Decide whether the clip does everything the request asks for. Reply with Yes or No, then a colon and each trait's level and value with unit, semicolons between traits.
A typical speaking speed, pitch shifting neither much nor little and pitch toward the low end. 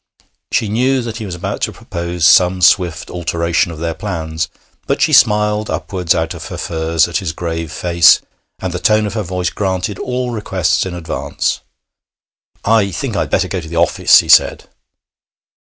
Yes: average, 180 wpm; average, 3.8 semitones; very low, 90 Hz